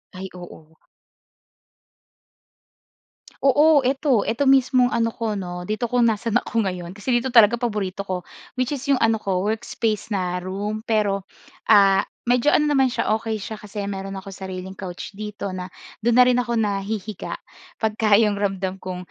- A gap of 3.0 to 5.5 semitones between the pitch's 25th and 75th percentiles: Yes, average, 3.6 semitones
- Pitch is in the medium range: No, high, 215 Hz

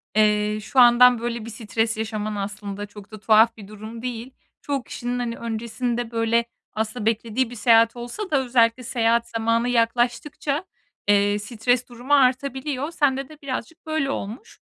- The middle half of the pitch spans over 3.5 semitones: No, narrow, 2.5 semitones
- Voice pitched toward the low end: No, high, 235 Hz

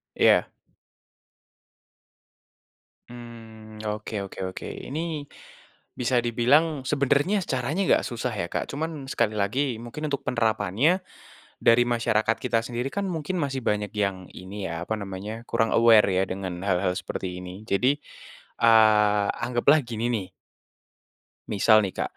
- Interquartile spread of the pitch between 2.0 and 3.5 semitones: No, average, 4.1 semitones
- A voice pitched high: No, low, 115 Hz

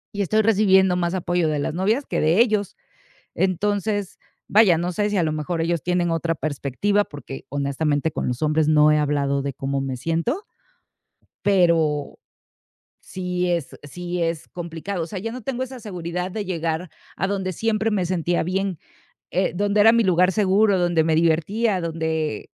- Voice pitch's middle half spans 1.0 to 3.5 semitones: No, average, 4.0 semitones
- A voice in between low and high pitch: Yes, medium, 175 Hz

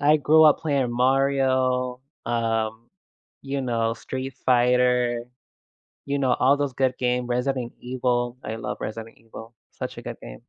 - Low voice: Yes, low, 125 Hz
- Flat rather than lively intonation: Yes, narrow, 2.1 semitones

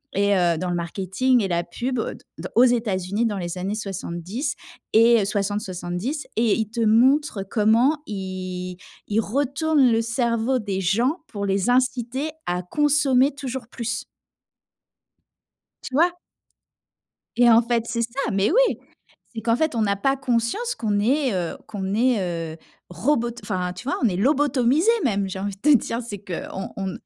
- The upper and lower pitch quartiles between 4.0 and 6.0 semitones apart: Yes, average, 4.9 semitones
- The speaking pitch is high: Yes, high, 225 Hz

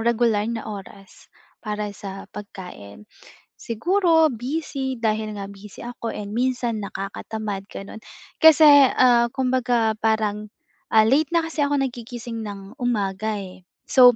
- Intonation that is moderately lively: Yes, average, 3.7 semitones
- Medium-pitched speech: No, high, 225 Hz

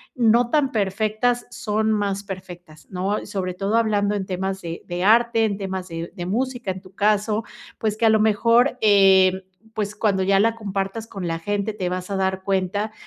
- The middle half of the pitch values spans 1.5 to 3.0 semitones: Yes, narrow, 2.5 semitones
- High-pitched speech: Yes, high, 200 Hz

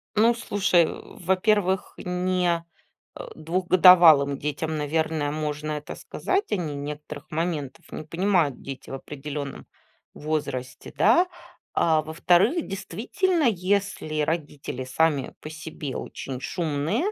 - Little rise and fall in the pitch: No, average, 4.0 semitones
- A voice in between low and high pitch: Yes, medium, 160 Hz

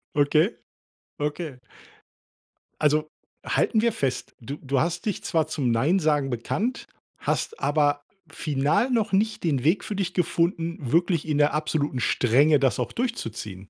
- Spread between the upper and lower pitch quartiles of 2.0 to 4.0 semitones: No, average, 4.4 semitones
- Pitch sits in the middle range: Yes, medium, 155 Hz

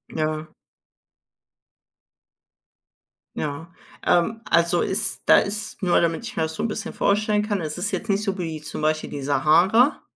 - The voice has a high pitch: No, medium, 175 Hz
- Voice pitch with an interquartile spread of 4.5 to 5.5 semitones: Yes, average, 5.0 semitones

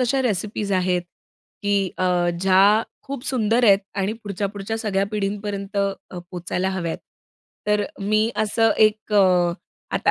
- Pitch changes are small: Yes, narrow, 2.2 semitones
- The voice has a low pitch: No, high, 200 Hz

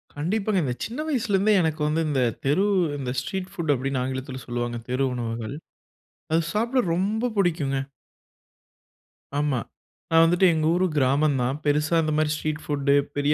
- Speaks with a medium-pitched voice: Yes, medium, 150 Hz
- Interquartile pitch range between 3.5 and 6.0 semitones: Yes, average, 5.0 semitones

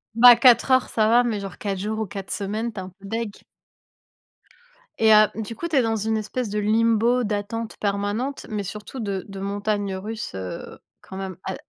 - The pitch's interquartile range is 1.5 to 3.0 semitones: Yes, narrow, 2.4 semitones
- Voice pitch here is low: No, high, 215 Hz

